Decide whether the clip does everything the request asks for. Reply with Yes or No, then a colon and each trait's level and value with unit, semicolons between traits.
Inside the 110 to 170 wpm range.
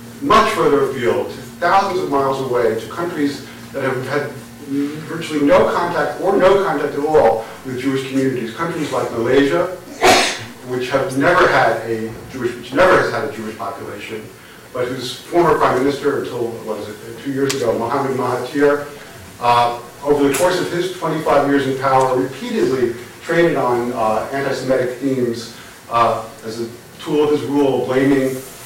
Yes: average, 155 wpm